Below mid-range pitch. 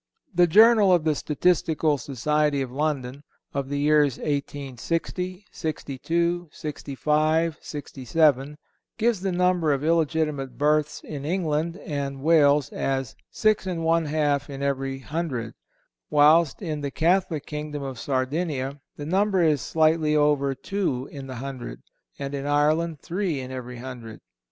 No: medium, 150 Hz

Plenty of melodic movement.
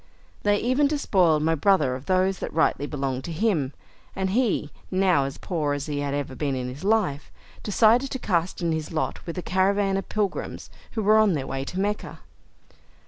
Yes: wide, 6.0 semitones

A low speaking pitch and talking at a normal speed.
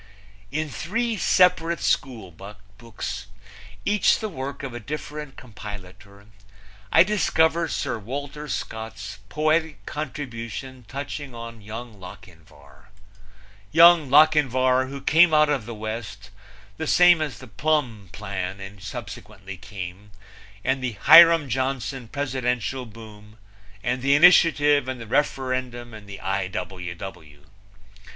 No: low, 125 Hz; slow, 115 wpm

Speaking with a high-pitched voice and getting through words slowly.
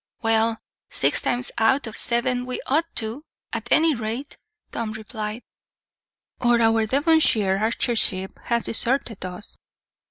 Yes: high, 230 Hz; slow, 125 wpm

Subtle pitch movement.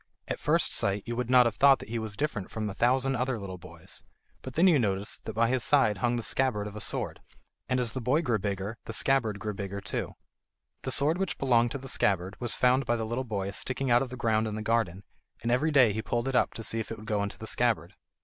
No: average, 3.6 semitones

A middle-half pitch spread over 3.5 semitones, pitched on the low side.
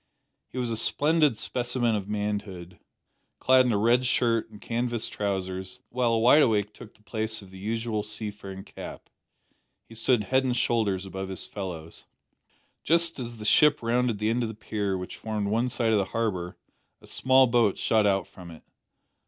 No: average, 3.2 semitones; low, 110 Hz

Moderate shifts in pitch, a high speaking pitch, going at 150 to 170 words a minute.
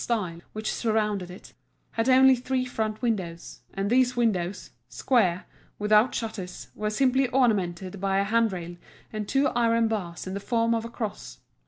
Yes: average, 3.7 semitones; high, 215 Hz; average, 160 wpm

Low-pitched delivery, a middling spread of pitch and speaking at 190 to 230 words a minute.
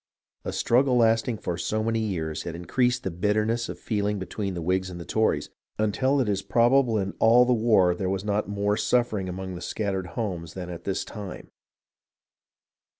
Yes: low, 105 Hz; average, 3.5 semitones; average, 195 wpm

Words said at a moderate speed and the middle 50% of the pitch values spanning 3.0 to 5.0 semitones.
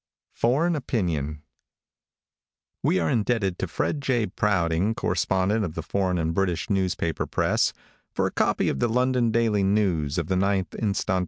Yes: average, 150 wpm; average, 4.6 semitones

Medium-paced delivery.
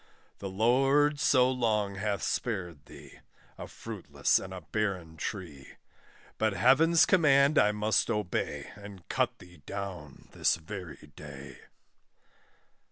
No: slow, 120 wpm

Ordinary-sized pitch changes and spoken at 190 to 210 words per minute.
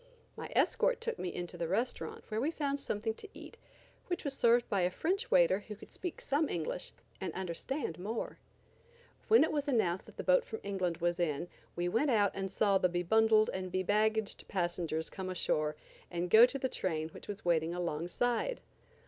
No: wide, 7.1 semitones; average, 195 wpm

